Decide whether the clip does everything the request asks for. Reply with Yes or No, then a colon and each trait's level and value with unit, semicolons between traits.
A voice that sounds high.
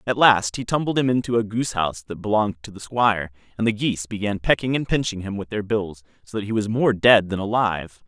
No: low, 105 Hz